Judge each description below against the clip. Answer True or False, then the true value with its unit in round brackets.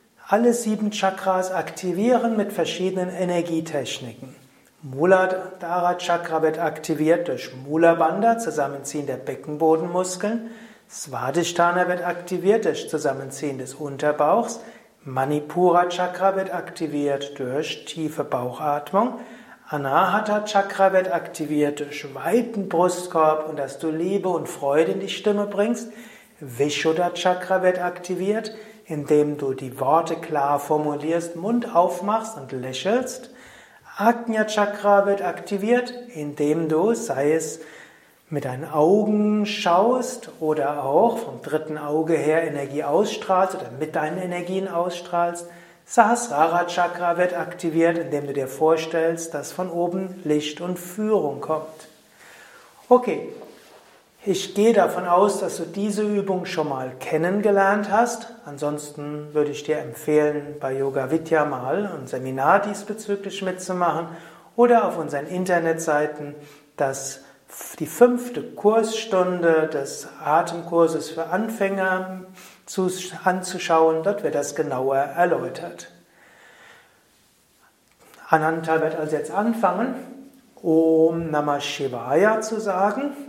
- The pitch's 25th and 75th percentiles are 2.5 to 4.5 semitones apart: False (5.0 semitones)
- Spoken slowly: True (110 wpm)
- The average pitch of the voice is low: False (175 Hz)